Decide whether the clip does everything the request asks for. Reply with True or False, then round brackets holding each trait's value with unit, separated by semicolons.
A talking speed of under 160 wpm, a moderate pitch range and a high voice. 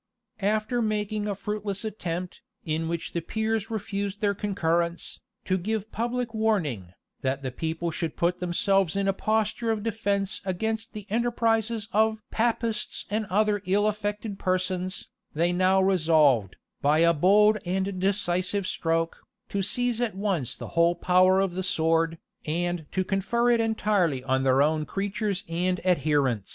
True (150 wpm; 4.0 semitones; 195 Hz)